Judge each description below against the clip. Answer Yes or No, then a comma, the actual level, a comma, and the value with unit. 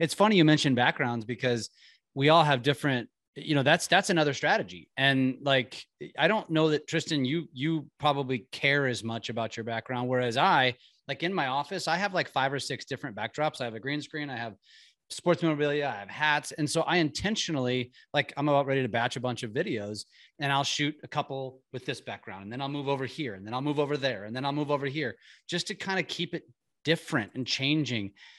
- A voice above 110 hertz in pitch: Yes, medium, 140 Hz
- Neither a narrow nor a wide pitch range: Yes, average, 3.7 semitones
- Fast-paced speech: Yes, fast, 225 wpm